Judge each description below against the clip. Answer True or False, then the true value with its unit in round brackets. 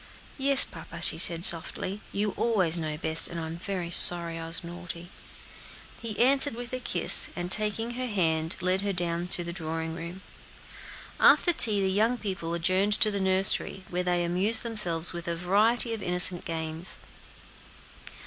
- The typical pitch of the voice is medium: True (180 Hz)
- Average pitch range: True (3.8 semitones)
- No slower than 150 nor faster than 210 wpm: True (170 wpm)